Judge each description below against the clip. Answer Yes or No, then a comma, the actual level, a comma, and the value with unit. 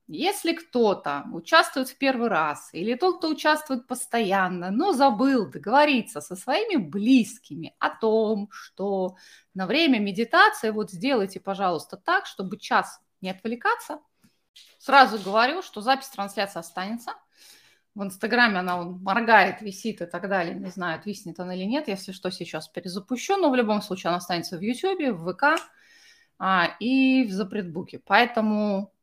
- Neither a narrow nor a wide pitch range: No, wide, 6.1 semitones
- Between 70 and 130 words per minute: No, average, 145 wpm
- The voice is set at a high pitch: Yes, high, 220 Hz